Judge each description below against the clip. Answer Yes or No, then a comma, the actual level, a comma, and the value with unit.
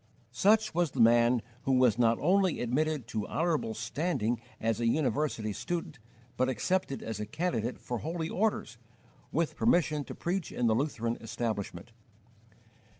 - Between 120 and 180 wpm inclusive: Yes, average, 150 wpm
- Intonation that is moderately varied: No, wide, 6.2 semitones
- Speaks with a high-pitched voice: No, low, 130 Hz